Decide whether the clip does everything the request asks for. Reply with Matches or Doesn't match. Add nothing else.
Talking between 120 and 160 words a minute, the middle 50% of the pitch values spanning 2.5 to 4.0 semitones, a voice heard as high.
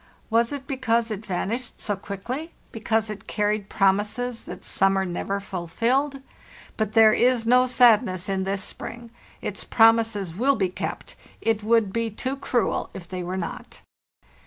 Matches